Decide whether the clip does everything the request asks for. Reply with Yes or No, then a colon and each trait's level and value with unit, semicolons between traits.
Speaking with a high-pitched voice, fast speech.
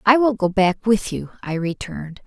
Yes: high, 200 Hz; fast, 210 wpm